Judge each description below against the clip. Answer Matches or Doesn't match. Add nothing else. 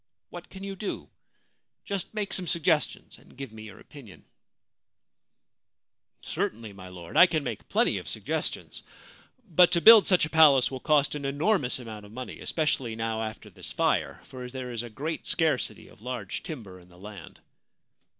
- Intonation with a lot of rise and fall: Matches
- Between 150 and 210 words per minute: Matches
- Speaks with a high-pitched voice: Doesn't match